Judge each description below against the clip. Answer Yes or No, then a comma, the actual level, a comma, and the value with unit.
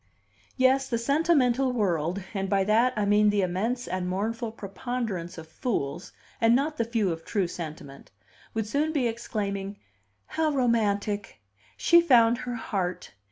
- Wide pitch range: No, average, 4.3 semitones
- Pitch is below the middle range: No, high, 220 Hz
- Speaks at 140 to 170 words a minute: Yes, average, 150 wpm